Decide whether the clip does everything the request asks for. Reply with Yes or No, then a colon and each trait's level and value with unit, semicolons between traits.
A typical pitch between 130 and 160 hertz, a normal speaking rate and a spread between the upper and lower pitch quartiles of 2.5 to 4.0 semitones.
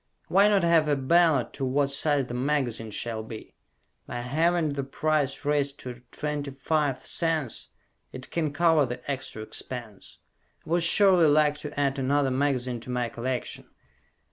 Yes: medium, 140 Hz; average, 155 wpm; average, 3.4 semitones